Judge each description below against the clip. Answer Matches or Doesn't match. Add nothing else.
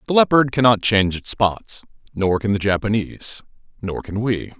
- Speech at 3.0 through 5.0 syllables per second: Doesn't match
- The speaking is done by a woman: Doesn't match